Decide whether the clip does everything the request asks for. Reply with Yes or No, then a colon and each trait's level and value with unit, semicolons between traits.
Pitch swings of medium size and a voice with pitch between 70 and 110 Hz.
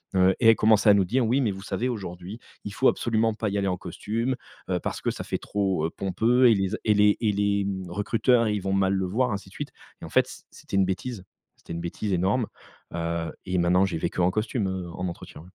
Yes: average, 3.2 semitones; low, 100 Hz